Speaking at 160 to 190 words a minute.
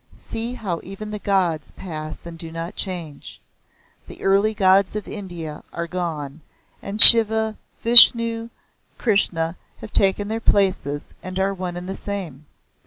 No: average, 145 wpm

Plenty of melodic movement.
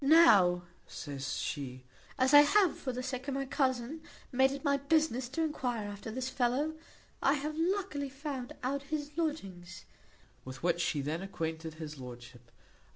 Yes: wide, 8.9 semitones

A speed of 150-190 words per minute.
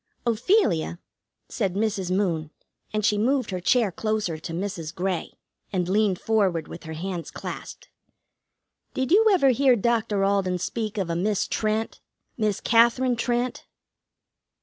No: average, 140 wpm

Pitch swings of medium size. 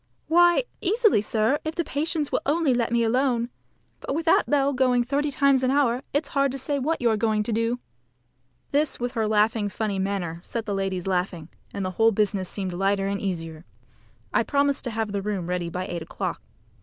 No: wide, 6.2 semitones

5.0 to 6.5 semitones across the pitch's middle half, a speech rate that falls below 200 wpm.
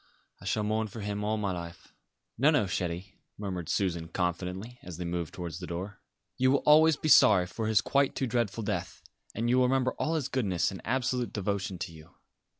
No: wide, 5.6 semitones; fast, 205 wpm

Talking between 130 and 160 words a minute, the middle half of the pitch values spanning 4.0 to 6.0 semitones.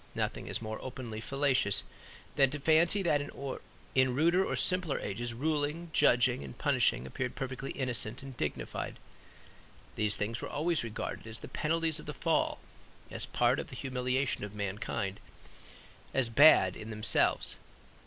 Yes: average, 150 wpm; average, 5.1 semitones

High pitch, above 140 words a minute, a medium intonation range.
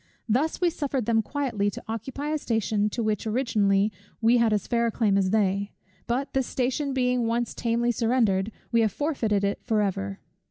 Yes: high, 230 Hz; average, 190 wpm; average, 3.3 semitones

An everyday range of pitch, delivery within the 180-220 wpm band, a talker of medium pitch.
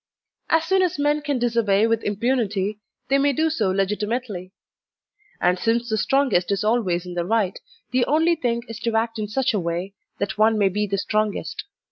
No: average, 4.4 semitones; average, 190 wpm; high, 220 Hz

